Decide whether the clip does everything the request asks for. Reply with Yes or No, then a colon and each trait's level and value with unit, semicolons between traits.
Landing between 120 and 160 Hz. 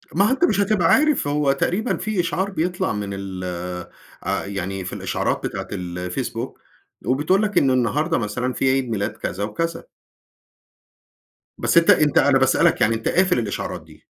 Yes: medium, 140 Hz